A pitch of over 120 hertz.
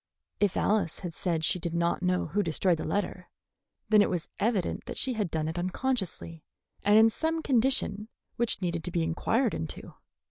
Yes: medium, 185 Hz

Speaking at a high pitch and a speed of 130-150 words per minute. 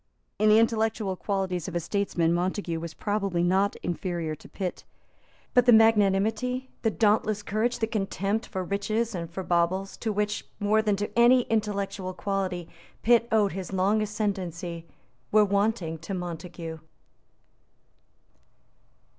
Yes: high, 200 Hz; average, 140 wpm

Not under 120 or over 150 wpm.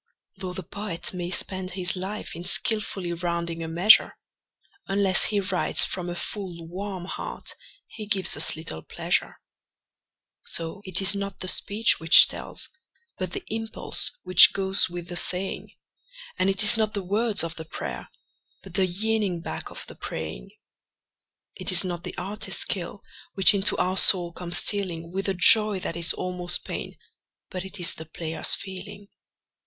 No: average, 165 wpm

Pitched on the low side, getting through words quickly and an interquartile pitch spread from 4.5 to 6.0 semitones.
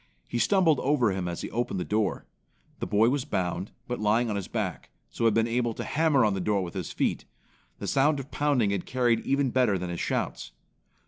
Yes: low, 115 Hz; fast, 220 wpm; average, 5.0 semitones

